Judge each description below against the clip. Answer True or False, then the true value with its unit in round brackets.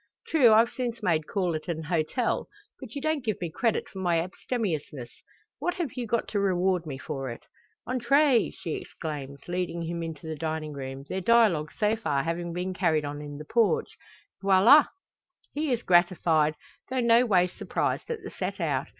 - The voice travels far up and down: True (6.9 semitones)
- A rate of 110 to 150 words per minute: False (185 wpm)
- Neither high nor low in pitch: True (180 Hz)